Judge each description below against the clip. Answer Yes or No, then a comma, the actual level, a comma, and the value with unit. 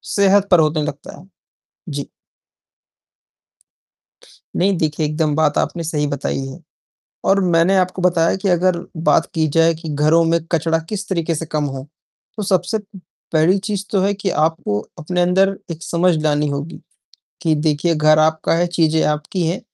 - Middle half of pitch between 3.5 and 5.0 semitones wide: No, average, 3.0 semitones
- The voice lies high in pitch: No, medium, 165 Hz